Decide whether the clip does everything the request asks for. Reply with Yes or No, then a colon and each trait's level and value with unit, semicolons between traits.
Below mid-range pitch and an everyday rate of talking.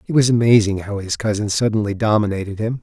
Yes: low, 110 Hz; average, 190 wpm